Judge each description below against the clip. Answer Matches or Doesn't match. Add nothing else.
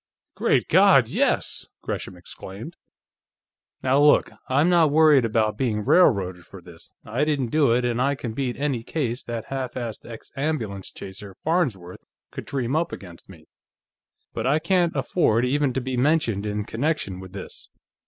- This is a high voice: Doesn't match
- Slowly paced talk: Doesn't match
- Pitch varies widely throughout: Matches